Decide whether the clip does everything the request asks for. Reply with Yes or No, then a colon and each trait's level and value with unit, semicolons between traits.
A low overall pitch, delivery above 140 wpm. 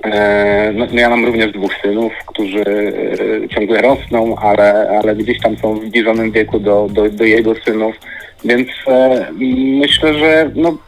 Yes: low, 110 Hz; average, 155 wpm